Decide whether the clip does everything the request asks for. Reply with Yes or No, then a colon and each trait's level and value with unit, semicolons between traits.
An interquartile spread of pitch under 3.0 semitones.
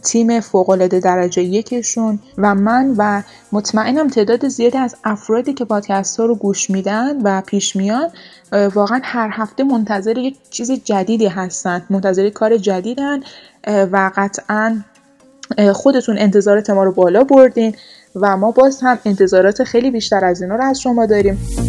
No: average, 3.6 semitones